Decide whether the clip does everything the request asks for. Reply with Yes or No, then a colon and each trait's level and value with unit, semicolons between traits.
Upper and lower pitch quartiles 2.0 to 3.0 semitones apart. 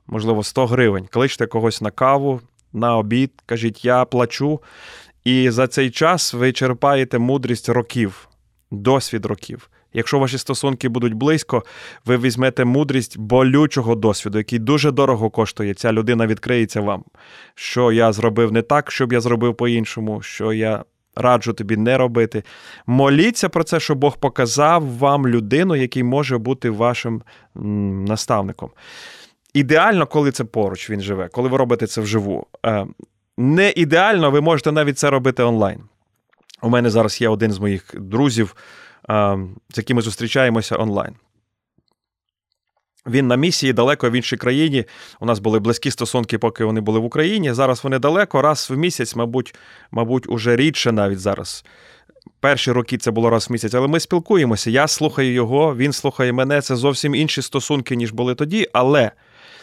No: average, 3.5 semitones